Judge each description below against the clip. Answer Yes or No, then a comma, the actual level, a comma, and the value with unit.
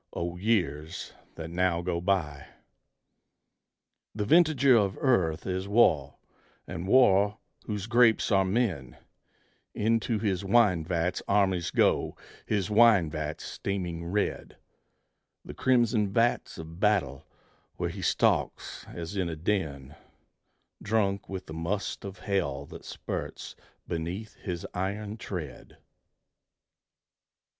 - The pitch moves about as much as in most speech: Yes, average, 4.0 semitones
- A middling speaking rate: No, slow, 115 wpm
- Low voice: Yes, very low, 95 Hz